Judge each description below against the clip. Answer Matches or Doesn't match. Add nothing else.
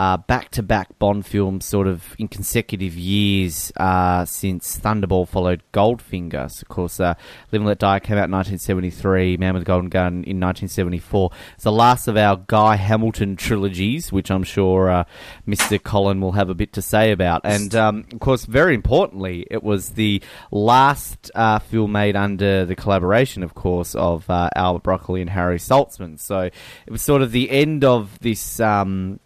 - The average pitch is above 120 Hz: Doesn't match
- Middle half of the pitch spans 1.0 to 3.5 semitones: Matches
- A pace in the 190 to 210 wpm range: Doesn't match